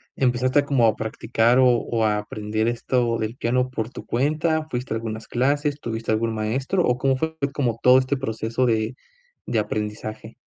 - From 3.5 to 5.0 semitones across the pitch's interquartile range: No, average, 2.8 semitones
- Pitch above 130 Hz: No, low, 120 Hz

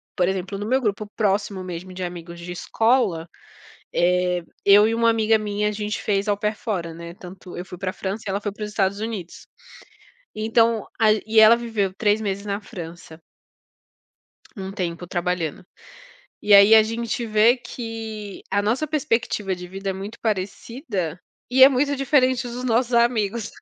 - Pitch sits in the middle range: No, high, 210 Hz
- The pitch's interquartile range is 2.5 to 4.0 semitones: Yes, average, 3.4 semitones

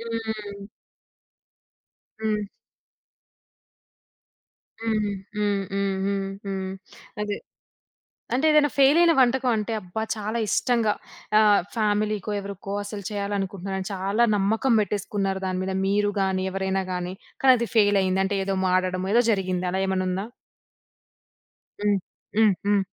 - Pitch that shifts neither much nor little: No, narrow, 2.2 semitones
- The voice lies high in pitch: Yes, high, 200 Hz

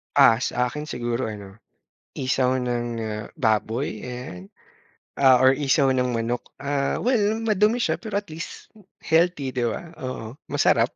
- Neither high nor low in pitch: No, low, 130 Hz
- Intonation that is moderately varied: Yes, average, 4.6 semitones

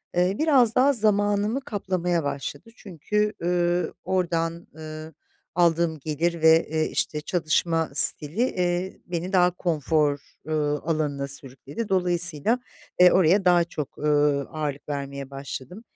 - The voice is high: No, medium, 170 Hz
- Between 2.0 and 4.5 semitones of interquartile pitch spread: Yes, average, 3.4 semitones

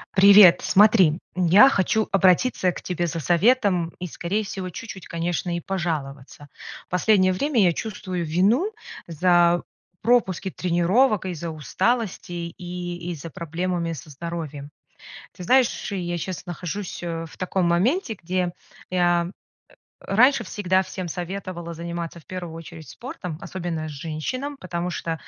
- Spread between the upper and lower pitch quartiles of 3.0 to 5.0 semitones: No, narrow, 2.6 semitones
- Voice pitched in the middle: Yes, medium, 180 Hz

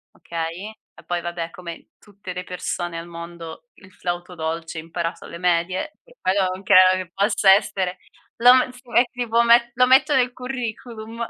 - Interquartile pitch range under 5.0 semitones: No, wide, 5.5 semitones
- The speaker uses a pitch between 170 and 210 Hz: Yes, medium, 185 Hz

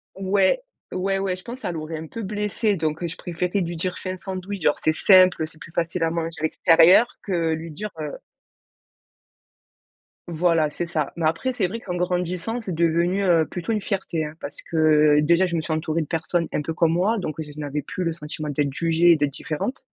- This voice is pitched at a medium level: Yes, medium, 170 Hz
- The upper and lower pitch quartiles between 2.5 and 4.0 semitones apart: Yes, average, 2.9 semitones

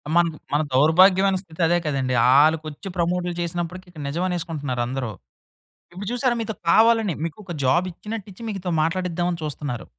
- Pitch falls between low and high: Yes, medium, 175 Hz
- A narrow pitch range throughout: No, average, 3.5 semitones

